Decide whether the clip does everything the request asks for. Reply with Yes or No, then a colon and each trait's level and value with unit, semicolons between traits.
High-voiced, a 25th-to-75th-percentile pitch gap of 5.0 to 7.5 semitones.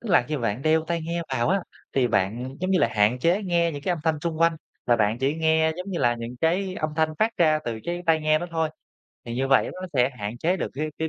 No: medium, 155 Hz; average, 5.3 semitones